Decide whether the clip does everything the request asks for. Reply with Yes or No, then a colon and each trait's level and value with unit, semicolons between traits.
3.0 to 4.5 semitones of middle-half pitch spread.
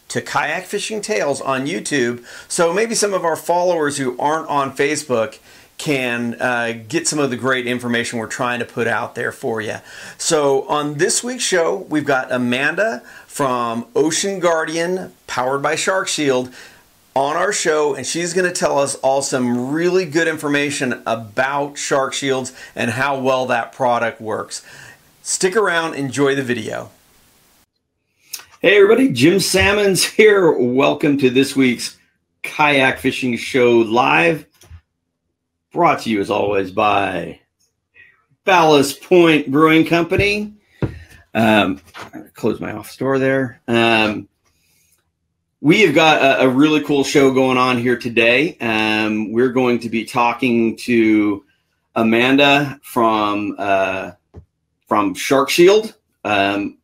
No: average, 4.9 semitones